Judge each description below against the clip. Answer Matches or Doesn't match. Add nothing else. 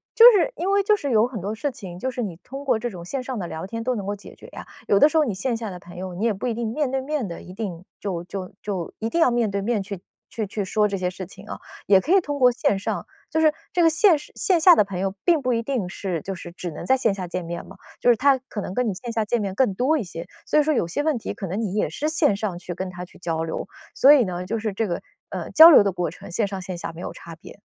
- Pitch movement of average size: Doesn't match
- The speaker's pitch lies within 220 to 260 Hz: Doesn't match